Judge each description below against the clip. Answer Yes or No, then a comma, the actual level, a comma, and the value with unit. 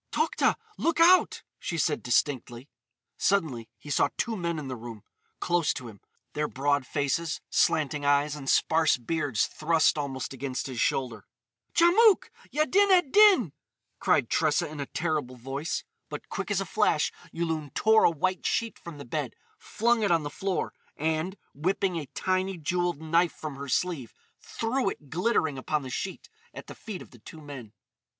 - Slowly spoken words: No, average, 170 wpm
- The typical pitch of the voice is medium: Yes, medium, 155 Hz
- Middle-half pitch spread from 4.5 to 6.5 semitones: Yes, average, 5.2 semitones